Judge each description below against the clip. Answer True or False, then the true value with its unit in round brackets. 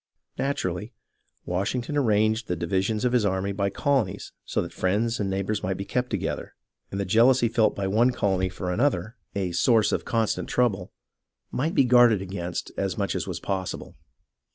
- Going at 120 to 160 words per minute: False (175 wpm)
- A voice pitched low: True (105 Hz)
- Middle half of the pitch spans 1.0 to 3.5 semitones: False (4.1 semitones)